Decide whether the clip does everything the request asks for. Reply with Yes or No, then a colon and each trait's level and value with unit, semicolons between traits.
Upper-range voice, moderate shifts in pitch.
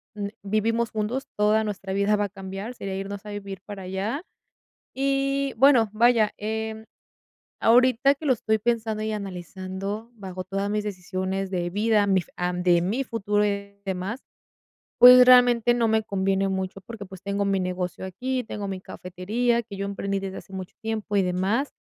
Yes: high, 205 Hz; average, 3.0 semitones